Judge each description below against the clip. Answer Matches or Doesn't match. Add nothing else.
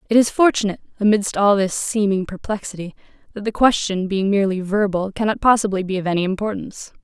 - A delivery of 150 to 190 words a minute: Matches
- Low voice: Doesn't match